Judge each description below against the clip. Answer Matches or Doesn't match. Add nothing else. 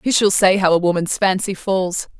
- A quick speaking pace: Matches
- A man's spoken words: Doesn't match